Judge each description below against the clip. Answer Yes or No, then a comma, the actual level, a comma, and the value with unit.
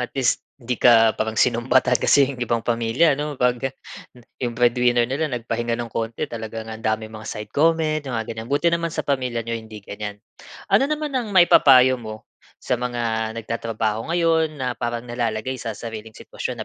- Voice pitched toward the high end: No, low, 120 Hz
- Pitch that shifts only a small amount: No, average, 3.1 semitones